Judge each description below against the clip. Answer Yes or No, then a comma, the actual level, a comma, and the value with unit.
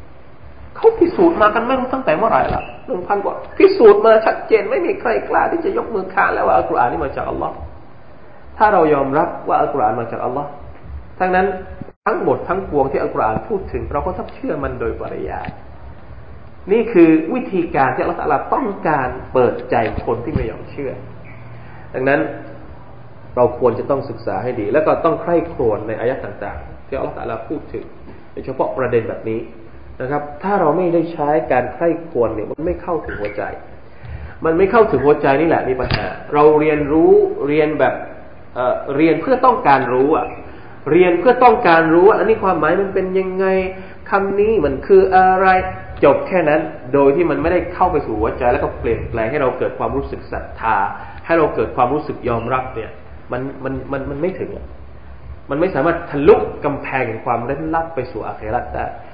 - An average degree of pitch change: No, wide, 7.1 semitones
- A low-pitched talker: No, medium, 160 Hz